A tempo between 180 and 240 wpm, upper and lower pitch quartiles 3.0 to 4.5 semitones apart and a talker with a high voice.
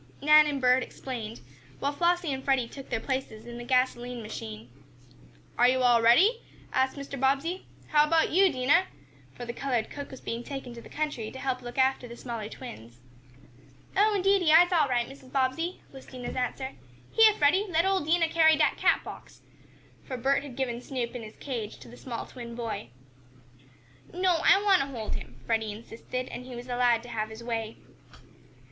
Yes: average, 190 wpm; average, 4.2 semitones; very high, 260 Hz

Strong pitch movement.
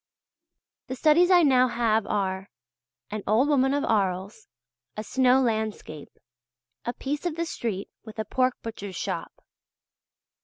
No: average, 4.2 semitones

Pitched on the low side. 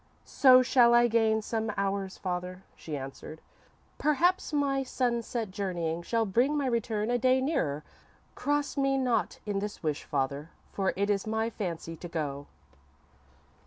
No: high, 220 Hz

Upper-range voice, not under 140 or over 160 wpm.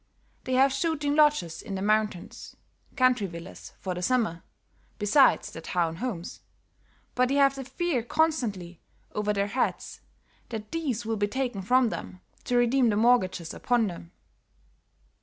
Yes: high, 225 Hz; average, 150 wpm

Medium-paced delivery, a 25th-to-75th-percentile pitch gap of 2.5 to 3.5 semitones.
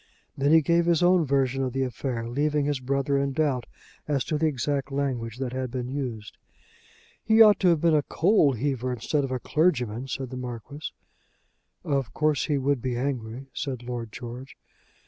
Yes: average, 185 wpm; average, 3.0 semitones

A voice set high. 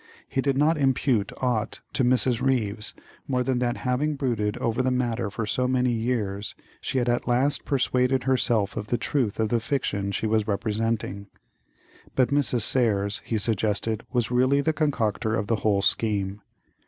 No: low, 120 Hz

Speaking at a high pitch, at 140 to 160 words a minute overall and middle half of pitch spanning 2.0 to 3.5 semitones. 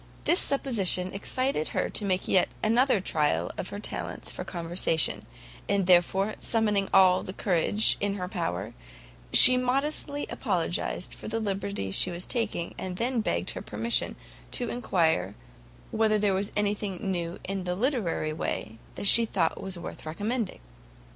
No: high, 195 Hz; average, 150 wpm; average, 4.2 semitones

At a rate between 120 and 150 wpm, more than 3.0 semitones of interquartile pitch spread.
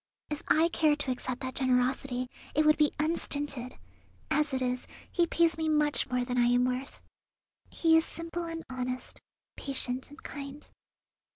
No: average, 165 wpm; average, 3.5 semitones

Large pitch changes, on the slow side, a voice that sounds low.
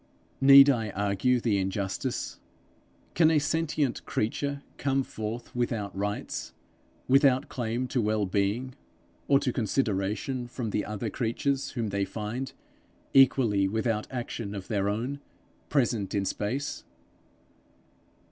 No: average, 4.6 semitones; slow, 120 wpm; low, 115 Hz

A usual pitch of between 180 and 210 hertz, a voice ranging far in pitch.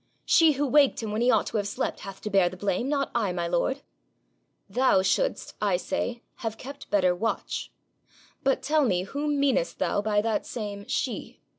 No: high, 225 Hz; wide, 5.7 semitones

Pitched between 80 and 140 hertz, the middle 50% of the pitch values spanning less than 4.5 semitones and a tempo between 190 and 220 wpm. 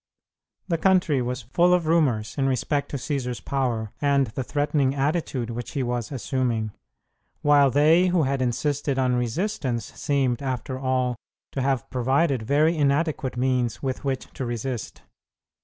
No: low, 135 Hz; average, 2.9 semitones; average, 150 wpm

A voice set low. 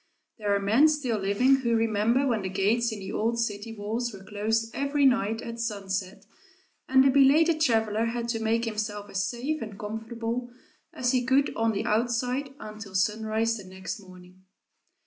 No: high, 225 Hz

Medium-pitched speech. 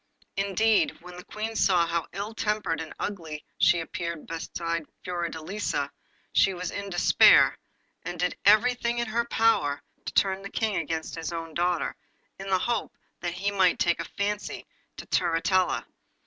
Yes: medium, 180 Hz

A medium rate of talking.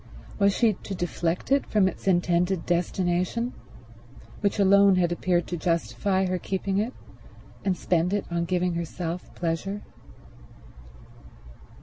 No: slow, 125 wpm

